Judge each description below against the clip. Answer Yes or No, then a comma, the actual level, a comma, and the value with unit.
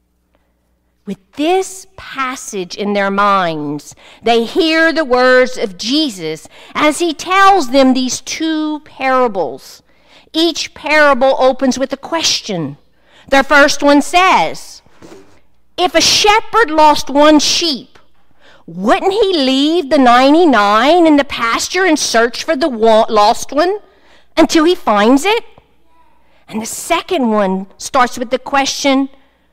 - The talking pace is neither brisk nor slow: No, slow, 125 wpm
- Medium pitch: No, very high, 275 Hz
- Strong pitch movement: Yes, wide, 6.0 semitones